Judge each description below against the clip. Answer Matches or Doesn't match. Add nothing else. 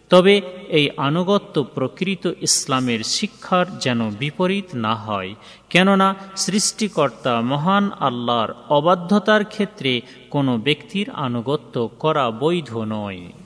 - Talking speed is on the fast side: Doesn't match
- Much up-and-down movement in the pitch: Matches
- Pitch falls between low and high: Matches